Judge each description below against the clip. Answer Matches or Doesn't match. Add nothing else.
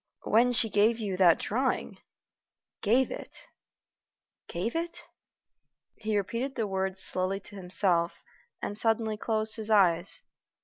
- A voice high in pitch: Matches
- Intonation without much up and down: Doesn't match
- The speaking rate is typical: Doesn't match